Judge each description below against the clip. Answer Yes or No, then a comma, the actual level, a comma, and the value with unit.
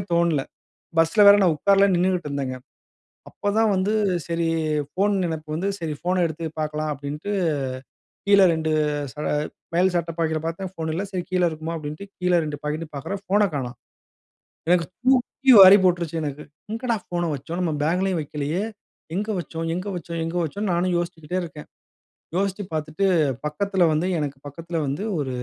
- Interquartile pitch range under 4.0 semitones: Yes, average, 3.6 semitones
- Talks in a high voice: No, medium, 170 Hz